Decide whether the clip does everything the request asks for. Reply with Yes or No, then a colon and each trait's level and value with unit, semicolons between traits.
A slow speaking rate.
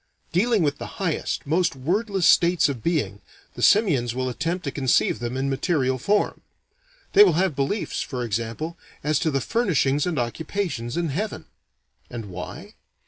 No: average, 160 wpm